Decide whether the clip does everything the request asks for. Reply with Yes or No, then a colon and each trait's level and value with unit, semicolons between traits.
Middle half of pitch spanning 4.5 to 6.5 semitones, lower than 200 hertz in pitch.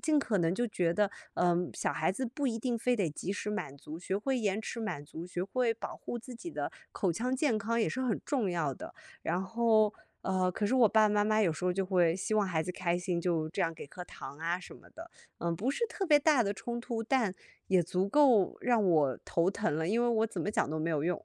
No: average, 5.2 semitones; high, 205 Hz